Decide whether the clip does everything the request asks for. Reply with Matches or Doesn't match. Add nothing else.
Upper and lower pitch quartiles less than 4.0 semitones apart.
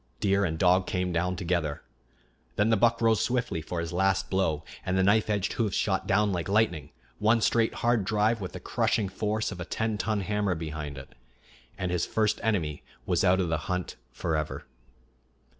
Matches